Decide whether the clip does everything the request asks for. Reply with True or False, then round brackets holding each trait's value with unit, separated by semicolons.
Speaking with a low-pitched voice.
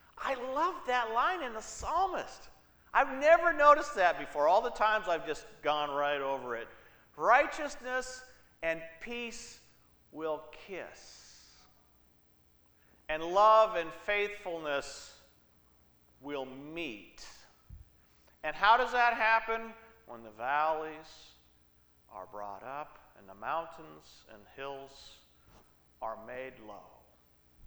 False (145 Hz)